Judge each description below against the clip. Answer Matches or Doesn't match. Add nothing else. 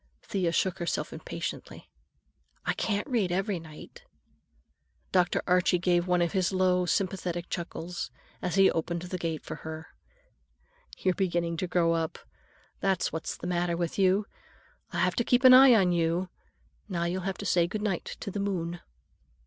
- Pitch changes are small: Matches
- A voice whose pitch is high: Doesn't match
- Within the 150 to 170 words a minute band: Matches